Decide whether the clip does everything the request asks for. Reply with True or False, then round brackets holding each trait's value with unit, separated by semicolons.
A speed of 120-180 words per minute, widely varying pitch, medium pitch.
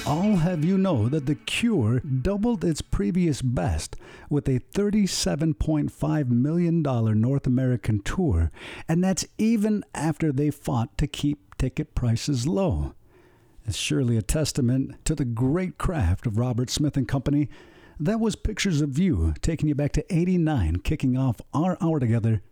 True (165 wpm; 5.7 semitones; 145 Hz)